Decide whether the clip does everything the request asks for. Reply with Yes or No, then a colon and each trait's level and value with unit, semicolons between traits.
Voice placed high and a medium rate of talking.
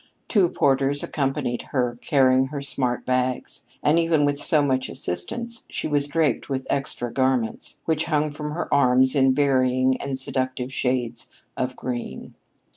No: low, 135 Hz; average, 150 wpm